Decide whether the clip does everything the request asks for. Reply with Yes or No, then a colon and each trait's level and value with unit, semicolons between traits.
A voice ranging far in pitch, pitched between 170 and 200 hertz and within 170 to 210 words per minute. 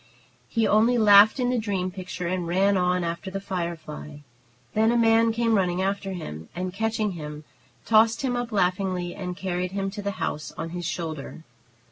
No: average, 3.7 semitones; high, 190 Hz; average, 180 wpm